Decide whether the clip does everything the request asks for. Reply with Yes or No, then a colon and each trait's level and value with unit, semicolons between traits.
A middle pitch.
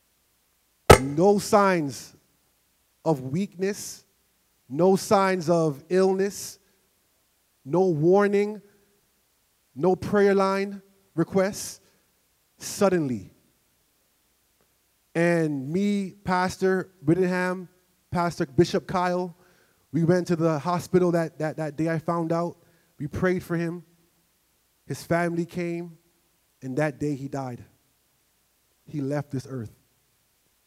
Yes: medium, 170 Hz